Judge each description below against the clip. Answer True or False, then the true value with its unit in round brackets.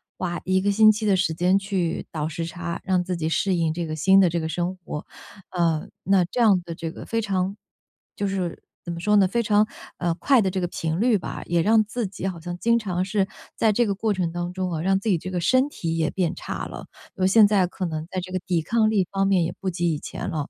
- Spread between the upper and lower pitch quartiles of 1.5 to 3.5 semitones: True (2.9 semitones)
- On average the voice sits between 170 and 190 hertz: True (185 Hz)